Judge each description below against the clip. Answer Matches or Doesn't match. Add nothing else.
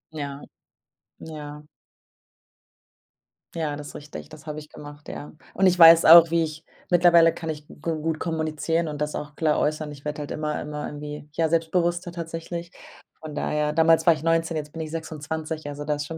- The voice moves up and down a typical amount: Doesn't match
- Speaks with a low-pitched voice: Doesn't match